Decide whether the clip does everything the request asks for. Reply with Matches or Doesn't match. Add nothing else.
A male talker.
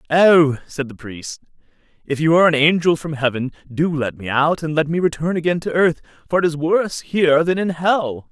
Matches